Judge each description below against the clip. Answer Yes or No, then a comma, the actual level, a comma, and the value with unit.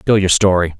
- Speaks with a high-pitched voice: No, very low, 95 Hz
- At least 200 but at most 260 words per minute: Yes, fast, 225 wpm